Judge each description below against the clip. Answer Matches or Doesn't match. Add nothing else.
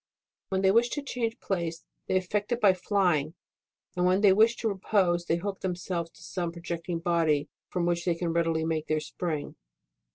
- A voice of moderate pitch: Matches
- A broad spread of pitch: Doesn't match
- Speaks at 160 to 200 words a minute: Matches